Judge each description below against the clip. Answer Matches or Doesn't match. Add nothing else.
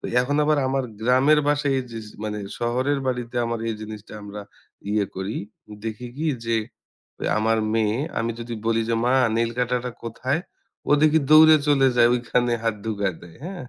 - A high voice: Doesn't match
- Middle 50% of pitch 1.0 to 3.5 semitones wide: Matches